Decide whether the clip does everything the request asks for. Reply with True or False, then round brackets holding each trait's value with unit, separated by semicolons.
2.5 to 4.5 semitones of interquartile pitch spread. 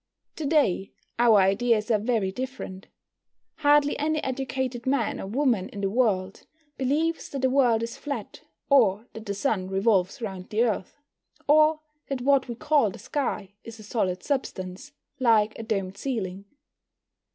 False (5.5 semitones)